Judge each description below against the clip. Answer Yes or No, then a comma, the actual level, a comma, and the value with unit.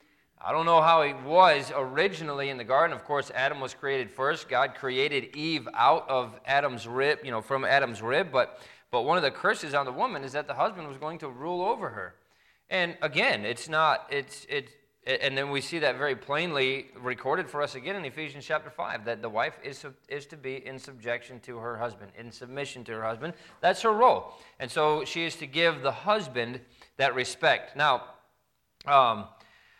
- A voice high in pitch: No, medium, 140 Hz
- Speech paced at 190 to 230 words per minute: Yes, fast, 205 wpm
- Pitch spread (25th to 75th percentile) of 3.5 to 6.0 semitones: Yes, average, 4.0 semitones